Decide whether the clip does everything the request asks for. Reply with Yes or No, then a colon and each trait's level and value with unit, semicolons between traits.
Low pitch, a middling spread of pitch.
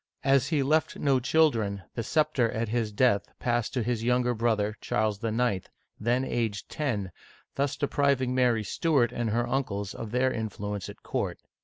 Yes: low, 120 Hz; average, 3.5 semitones